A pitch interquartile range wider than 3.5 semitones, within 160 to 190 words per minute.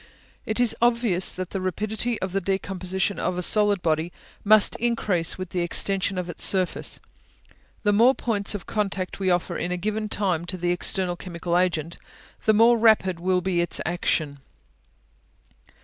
No: average, 3.0 semitones; average, 165 wpm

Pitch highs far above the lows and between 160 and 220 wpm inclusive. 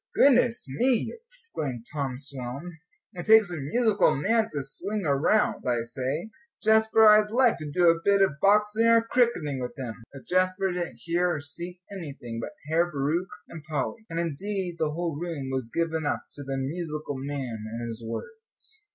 Yes: wide, 7.1 semitones; average, 175 wpm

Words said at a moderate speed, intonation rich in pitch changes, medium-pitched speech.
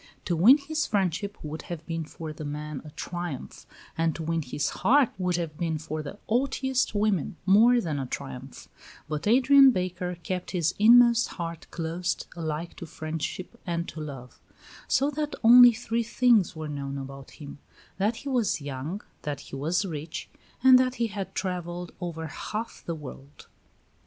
Yes: average, 170 wpm; wide, 6.3 semitones; medium, 175 Hz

